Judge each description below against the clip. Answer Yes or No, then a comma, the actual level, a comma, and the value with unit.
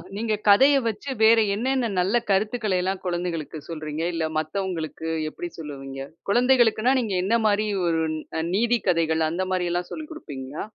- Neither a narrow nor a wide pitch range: No, wide, 5.7 semitones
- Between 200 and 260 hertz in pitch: No, high, 190 Hz